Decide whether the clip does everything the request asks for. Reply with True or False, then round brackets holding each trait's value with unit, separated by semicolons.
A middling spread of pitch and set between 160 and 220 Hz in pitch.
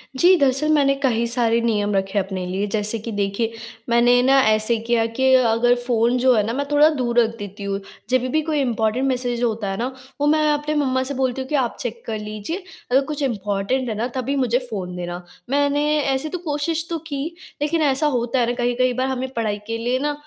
False (3.7 semitones; 245 Hz)